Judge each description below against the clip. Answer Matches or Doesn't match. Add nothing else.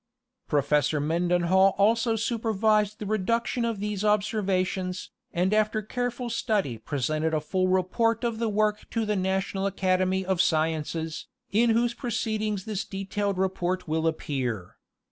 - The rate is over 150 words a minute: Doesn't match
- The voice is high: Matches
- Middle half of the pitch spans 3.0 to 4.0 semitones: Matches